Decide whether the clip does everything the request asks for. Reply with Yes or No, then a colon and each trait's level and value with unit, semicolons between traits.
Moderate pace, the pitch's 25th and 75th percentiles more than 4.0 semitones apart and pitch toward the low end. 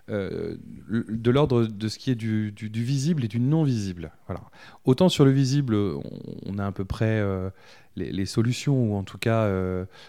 Yes: average, 200 wpm; average, 4.6 semitones; low, 110 Hz